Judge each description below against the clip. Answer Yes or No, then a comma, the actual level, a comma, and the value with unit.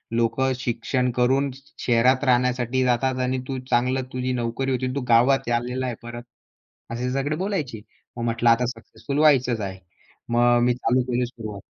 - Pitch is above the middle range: No, low, 125 Hz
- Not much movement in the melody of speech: Yes, narrow, 1.7 semitones